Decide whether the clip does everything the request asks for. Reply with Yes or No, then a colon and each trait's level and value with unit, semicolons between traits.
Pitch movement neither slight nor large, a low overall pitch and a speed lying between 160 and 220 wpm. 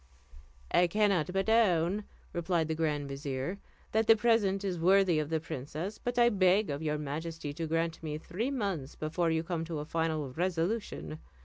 No: average, 4.2 semitones; medium, 165 Hz; average, 180 wpm